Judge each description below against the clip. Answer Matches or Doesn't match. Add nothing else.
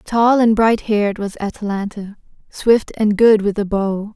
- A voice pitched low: Doesn't match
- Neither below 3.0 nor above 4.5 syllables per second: Matches